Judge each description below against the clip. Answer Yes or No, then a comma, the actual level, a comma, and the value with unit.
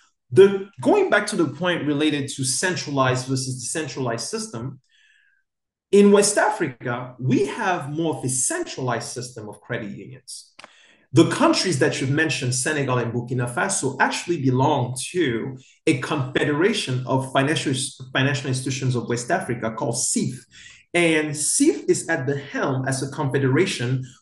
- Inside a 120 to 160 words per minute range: Yes, average, 140 wpm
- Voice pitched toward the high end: No, medium, 140 Hz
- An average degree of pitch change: Yes, average, 4.2 semitones